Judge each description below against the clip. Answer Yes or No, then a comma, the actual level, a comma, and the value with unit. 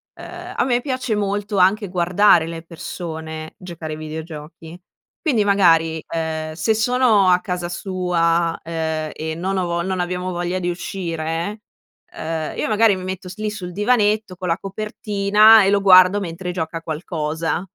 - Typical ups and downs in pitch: Yes, average, 3.6 semitones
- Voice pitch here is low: No, medium, 180 Hz